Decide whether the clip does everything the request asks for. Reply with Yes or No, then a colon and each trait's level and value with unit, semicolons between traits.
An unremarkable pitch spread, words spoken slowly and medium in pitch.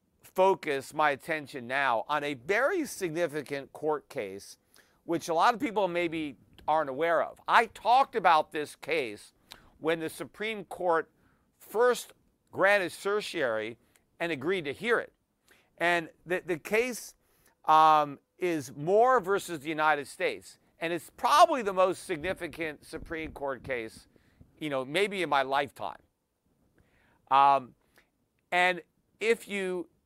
Yes: average, 5.0 semitones; slow, 130 wpm; medium, 165 Hz